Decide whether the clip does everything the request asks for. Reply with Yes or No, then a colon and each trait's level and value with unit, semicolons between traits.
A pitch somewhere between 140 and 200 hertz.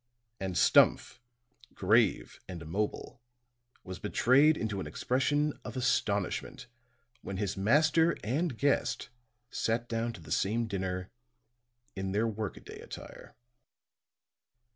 No: low, 110 Hz